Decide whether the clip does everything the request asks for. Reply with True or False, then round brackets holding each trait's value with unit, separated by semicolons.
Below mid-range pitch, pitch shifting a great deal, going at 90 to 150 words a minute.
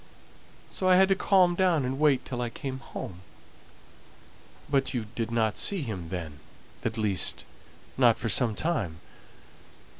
True (125 Hz; 7.4 semitones; 145 wpm)